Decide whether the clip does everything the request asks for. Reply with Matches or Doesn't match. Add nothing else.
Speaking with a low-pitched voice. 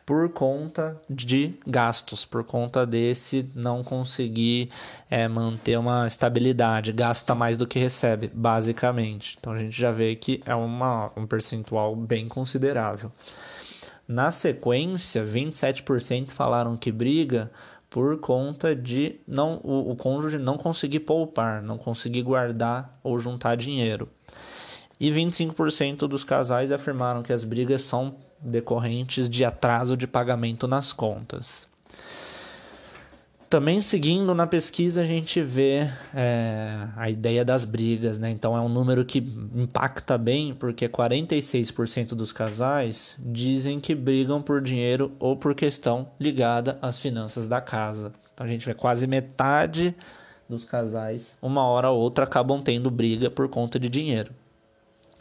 Matches